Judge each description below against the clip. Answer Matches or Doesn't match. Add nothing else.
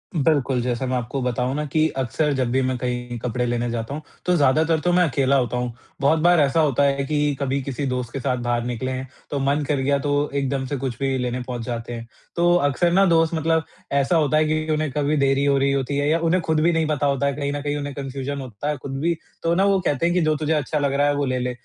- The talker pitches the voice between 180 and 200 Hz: Doesn't match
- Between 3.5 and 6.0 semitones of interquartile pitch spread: Doesn't match